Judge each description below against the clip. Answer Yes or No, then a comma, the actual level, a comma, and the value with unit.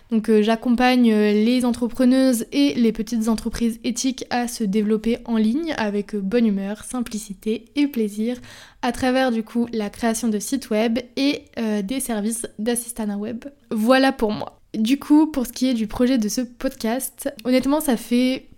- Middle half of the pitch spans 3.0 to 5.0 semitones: No, narrow, 2.6 semitones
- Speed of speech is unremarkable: Yes, average, 170 wpm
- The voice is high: Yes, high, 235 Hz